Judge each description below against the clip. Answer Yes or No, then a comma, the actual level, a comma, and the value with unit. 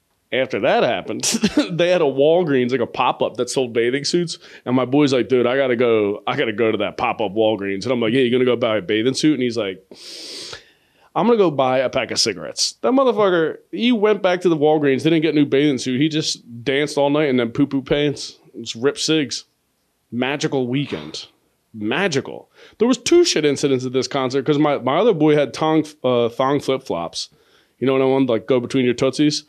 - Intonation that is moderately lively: Yes, average, 3.5 semitones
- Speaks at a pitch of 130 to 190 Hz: Yes, medium, 140 Hz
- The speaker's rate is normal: No, fast, 230 wpm